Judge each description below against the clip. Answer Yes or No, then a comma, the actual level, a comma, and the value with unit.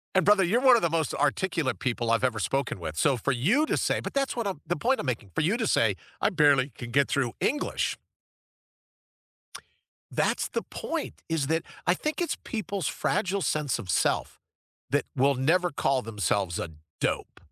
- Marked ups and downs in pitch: Yes, wide, 7.3 semitones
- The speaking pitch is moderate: Yes, medium, 150 Hz